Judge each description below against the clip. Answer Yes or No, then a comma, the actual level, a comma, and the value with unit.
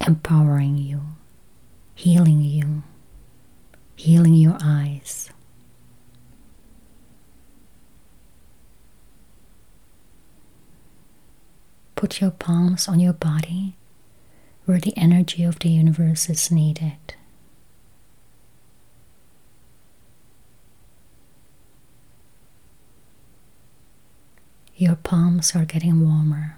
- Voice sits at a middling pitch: Yes, medium, 160 Hz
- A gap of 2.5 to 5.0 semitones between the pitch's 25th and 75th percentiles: Yes, average, 3.0 semitones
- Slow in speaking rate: Yes, slow, 60 wpm